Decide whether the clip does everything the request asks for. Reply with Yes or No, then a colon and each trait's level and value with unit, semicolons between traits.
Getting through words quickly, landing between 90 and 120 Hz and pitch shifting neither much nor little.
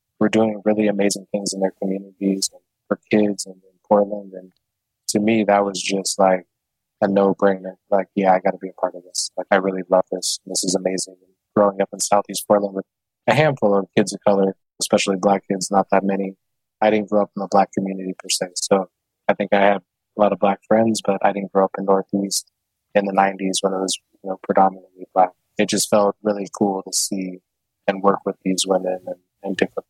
No: fast, 225 wpm; low, 100 Hz; narrow, 1.4 semitones